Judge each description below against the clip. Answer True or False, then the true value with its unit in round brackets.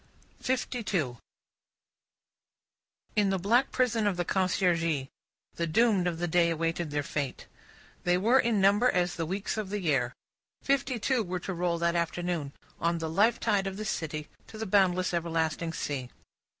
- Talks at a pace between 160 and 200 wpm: True (165 wpm)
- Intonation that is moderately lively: True (4.0 semitones)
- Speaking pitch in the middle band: True (180 Hz)